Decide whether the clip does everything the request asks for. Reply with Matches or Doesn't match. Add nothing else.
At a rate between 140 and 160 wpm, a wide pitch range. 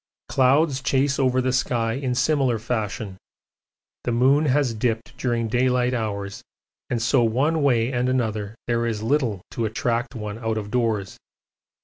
Doesn't match